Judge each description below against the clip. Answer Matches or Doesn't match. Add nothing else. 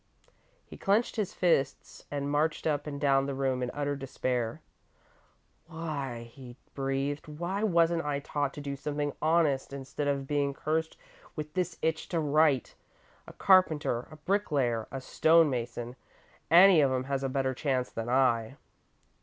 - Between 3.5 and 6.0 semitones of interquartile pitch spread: Doesn't match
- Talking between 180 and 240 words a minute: Doesn't match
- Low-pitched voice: Doesn't match